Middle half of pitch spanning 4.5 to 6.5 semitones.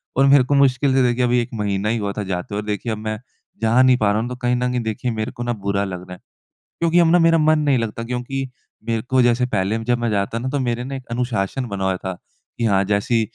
No: average, 3.5 semitones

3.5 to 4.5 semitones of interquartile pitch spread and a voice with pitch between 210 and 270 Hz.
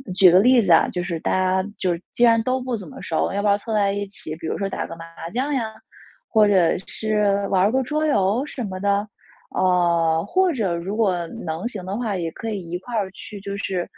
No: average, 4.0 semitones; high, 200 Hz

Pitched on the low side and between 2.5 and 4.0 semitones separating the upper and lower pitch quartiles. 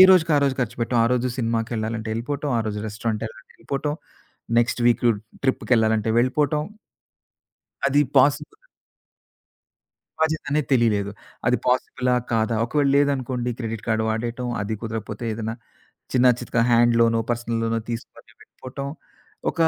Yes: low, 120 Hz; average, 2.8 semitones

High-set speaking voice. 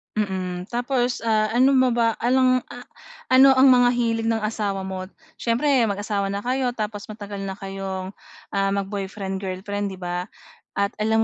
Yes: high, 210 Hz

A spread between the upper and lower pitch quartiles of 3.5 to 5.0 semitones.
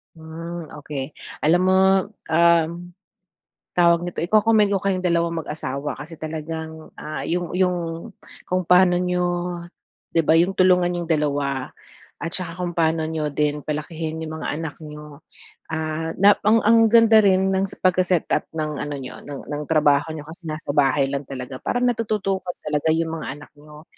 No: average, 3.1 semitones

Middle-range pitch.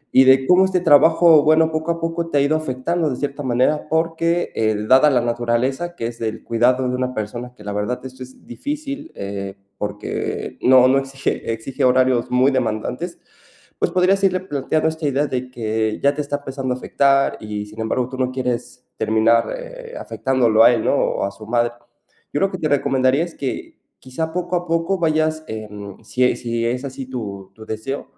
No: low, 130 Hz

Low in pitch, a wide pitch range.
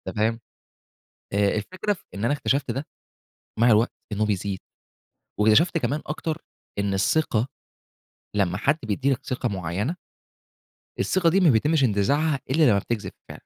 Yes: low, 120 Hz; wide, 6.6 semitones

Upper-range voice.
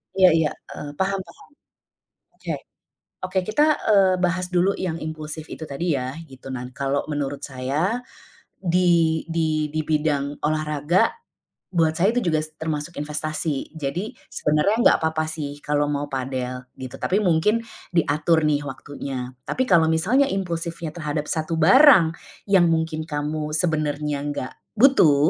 No: medium, 155 Hz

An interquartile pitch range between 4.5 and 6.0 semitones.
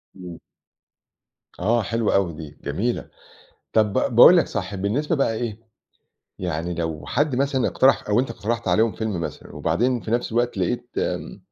Yes: average, 4.8 semitones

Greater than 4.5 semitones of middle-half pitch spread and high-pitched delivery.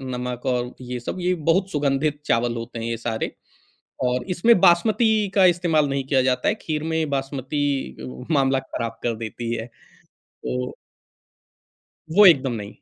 No: average, 5.1 semitones; low, 135 Hz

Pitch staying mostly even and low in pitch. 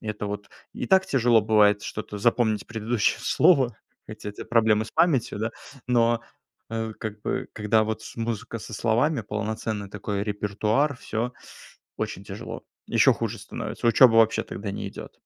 Yes: narrow, 2.0 semitones; low, 110 Hz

